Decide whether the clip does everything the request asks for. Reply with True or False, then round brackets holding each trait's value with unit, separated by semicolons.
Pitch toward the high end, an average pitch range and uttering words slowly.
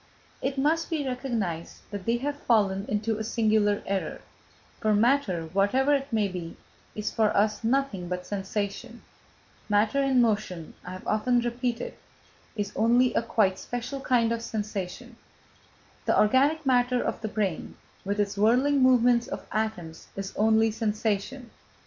False (220 Hz; 3.5 semitones; 150 wpm)